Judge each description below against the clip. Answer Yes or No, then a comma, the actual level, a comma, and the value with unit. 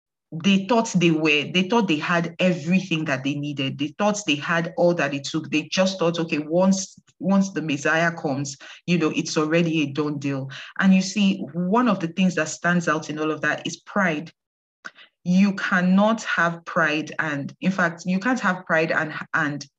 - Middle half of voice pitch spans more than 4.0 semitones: No, average, 3.4 semitones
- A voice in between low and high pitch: Yes, medium, 165 Hz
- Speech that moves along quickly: No, average, 195 wpm